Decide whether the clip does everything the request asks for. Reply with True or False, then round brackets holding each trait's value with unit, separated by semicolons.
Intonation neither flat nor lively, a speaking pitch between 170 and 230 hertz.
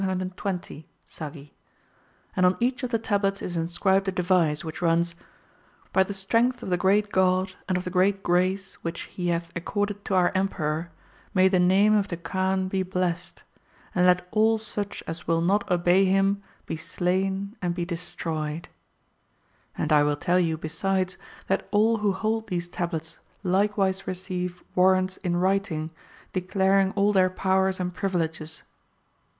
False (2.0 semitones; 185 Hz)